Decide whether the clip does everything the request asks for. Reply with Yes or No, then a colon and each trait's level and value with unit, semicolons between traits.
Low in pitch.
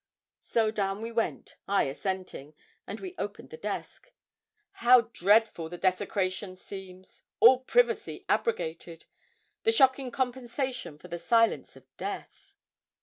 No: high, 215 Hz